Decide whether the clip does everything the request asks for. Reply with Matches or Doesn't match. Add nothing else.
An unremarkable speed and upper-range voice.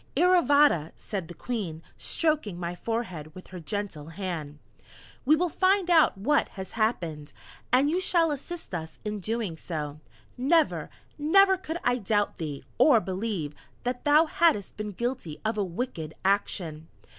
Matches